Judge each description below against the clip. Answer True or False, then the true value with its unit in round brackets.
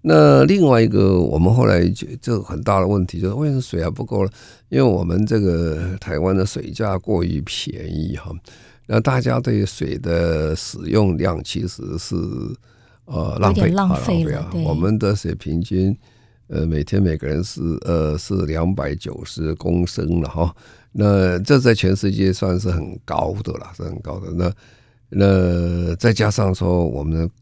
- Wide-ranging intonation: False (4.7 semitones)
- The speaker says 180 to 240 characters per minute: True (230 characters per minute)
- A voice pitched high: False (95 Hz)